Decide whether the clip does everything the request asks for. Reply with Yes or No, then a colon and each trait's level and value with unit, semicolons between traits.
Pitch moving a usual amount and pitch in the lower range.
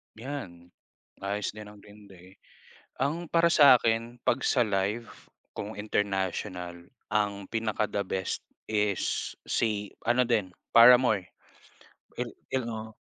Yes: average, 3.1 semitones; low, 105 Hz